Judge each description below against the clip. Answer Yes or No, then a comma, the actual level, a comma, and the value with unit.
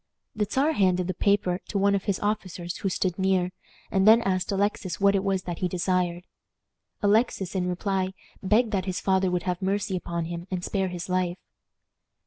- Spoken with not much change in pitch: Yes, narrow, 1.8 semitones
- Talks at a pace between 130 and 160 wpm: No, average, 190 wpm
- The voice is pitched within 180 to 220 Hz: Yes, high, 190 Hz